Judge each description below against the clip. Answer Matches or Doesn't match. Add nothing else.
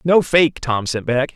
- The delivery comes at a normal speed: Doesn't match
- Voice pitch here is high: Doesn't match